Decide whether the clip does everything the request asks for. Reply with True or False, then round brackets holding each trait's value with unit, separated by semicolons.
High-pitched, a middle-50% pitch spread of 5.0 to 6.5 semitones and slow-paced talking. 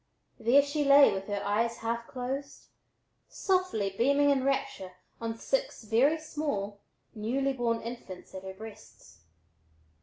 True (235 Hz; 5.4 semitones; 130 wpm)